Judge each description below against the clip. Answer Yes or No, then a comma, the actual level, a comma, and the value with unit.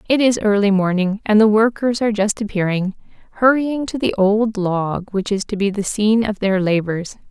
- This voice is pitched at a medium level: No, high, 210 Hz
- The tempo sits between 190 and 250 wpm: Yes, average, 195 wpm